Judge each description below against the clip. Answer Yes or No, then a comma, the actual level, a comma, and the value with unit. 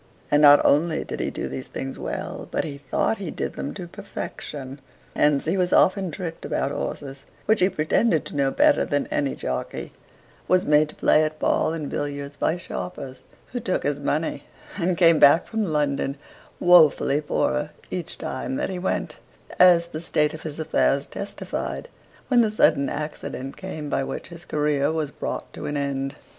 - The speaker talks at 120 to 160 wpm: No, average, 180 wpm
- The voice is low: No, medium, 150 Hz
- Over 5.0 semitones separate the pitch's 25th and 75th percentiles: No, average, 3.6 semitones